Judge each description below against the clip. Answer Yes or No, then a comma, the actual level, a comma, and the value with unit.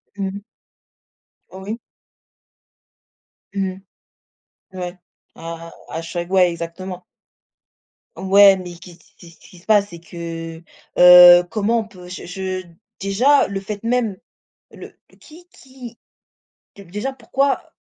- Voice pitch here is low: No, high, 190 Hz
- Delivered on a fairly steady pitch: No, average, 3.2 semitones